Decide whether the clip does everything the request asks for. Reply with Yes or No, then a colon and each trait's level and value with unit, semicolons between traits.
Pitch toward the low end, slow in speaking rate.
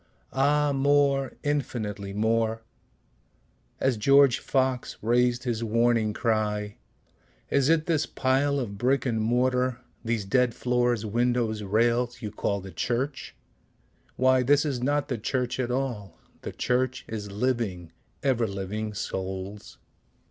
Yes: low, 120 Hz; slow, 125 wpm